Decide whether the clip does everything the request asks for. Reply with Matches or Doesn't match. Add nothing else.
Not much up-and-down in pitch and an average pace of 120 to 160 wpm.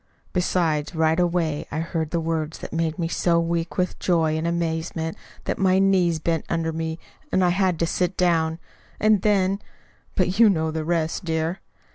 Doesn't match